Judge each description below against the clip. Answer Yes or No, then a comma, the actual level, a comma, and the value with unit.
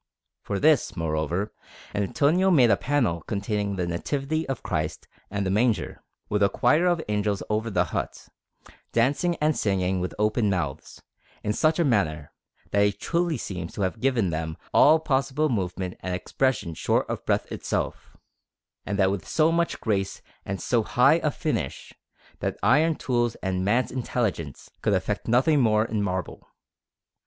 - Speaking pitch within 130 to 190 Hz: No, low, 105 Hz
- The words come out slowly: No, average, 160 wpm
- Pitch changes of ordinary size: No, wide, 6.4 semitones